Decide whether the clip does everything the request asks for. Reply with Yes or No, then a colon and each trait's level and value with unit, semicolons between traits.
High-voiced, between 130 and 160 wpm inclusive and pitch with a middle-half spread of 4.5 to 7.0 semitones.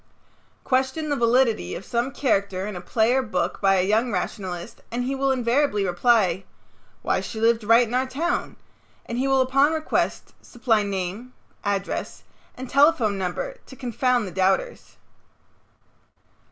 Yes: high, 235 Hz; average, 155 wpm; average, 4.9 semitones